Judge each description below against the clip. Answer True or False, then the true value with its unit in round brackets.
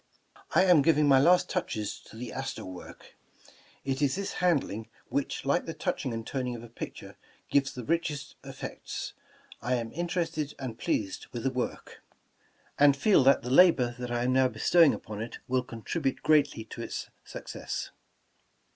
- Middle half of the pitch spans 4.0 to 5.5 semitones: True (4.3 semitones)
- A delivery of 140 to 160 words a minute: False (175 wpm)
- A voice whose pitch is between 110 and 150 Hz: True (135 Hz)